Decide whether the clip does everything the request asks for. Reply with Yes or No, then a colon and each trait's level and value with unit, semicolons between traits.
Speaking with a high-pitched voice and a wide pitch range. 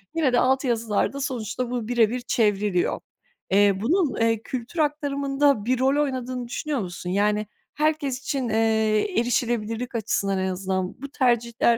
No: high, 240 Hz; average, 4.1 semitones